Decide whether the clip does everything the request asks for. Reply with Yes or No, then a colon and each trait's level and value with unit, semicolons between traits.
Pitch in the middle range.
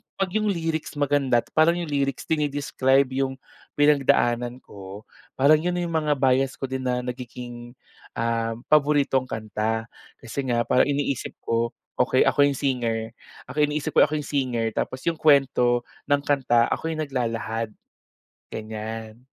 No: low, 130 Hz